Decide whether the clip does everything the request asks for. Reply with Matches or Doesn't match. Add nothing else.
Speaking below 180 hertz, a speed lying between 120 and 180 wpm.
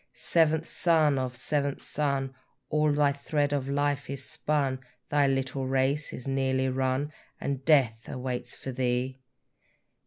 Matches